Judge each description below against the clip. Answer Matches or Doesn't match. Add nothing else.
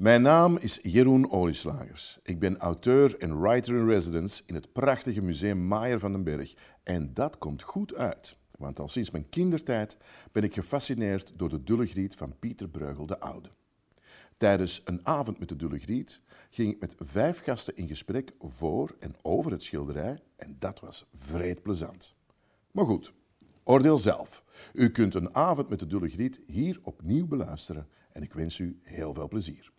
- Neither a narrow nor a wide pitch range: Doesn't match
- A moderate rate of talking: Matches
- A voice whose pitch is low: Matches